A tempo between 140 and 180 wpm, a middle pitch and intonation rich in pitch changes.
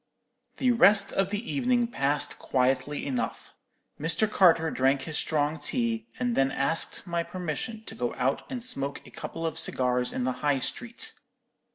Yes: average, 165 wpm; medium, 160 Hz; wide, 8.4 semitones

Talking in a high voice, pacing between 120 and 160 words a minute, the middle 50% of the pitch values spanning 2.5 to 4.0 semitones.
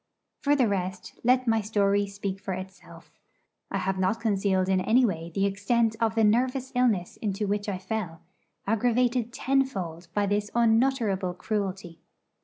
Yes: high, 205 Hz; average, 155 wpm; average, 3.5 semitones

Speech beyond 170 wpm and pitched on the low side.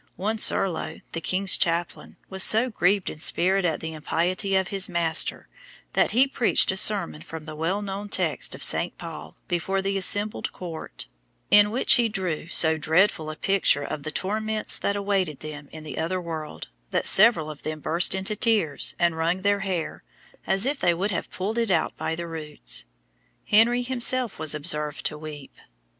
No: average, 180 wpm; medium, 185 Hz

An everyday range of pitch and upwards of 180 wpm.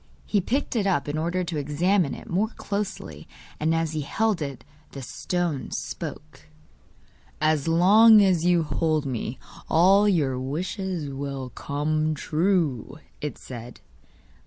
No: average, 4.7 semitones; slow, 135 wpm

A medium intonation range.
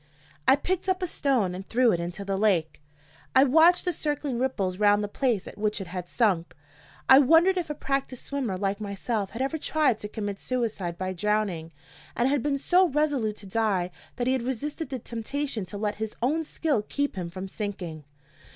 No: wide, 6.1 semitones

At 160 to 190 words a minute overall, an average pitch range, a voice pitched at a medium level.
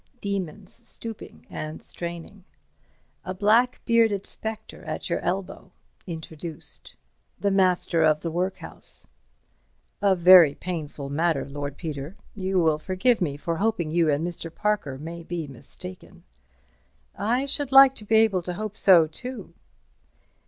No: slow, 135 wpm; average, 4.5 semitones; medium, 180 Hz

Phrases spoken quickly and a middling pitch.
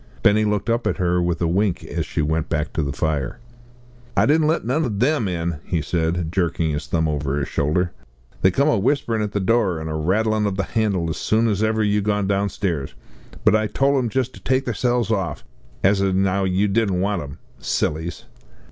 No: fast, 215 wpm; very low, 95 Hz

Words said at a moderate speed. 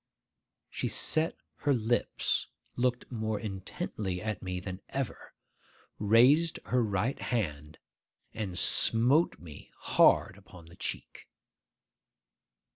No: slow, 105 wpm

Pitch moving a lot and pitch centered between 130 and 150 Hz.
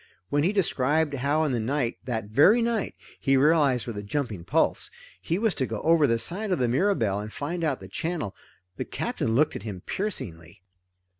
Yes: wide, 6.7 semitones; medium, 140 Hz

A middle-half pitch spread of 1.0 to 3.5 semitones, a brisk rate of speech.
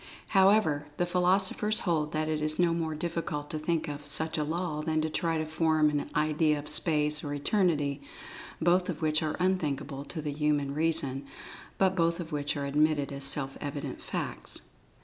No: narrow, 2.4 semitones; average, 185 wpm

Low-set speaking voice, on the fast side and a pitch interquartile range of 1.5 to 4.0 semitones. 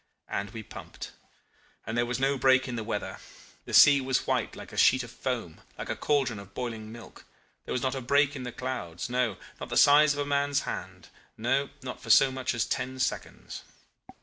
Yes: low, 130 Hz; fast, 210 wpm; average, 2.9 semitones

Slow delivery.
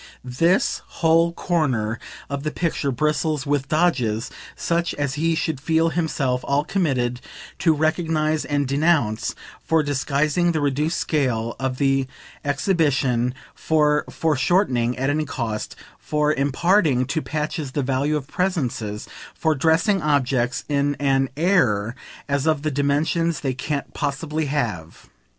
Yes: slow, 130 wpm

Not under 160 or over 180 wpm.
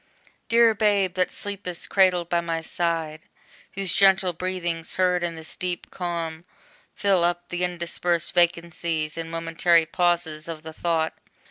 No: average, 140 wpm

